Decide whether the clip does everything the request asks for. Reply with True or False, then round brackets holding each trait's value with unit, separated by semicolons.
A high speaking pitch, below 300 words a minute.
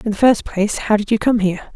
False (210 Hz; 310 wpm)